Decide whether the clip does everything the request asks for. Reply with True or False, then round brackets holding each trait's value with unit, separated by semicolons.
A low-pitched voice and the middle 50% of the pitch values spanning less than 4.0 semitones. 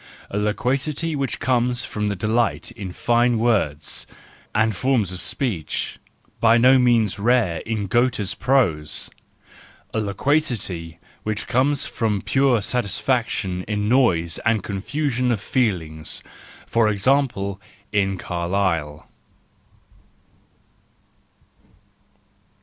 False (110 Hz; 4.5 semitones)